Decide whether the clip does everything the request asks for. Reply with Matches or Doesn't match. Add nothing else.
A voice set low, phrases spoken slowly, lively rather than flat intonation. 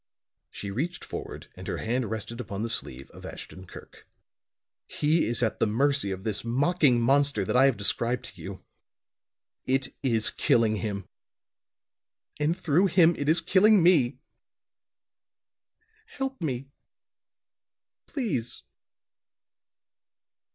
Matches